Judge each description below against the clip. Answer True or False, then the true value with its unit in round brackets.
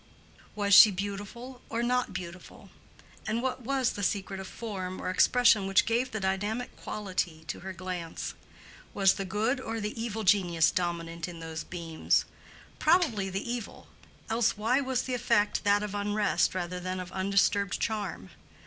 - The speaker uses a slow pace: False (160 wpm)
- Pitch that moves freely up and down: False (3.7 semitones)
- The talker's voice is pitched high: True (200 Hz)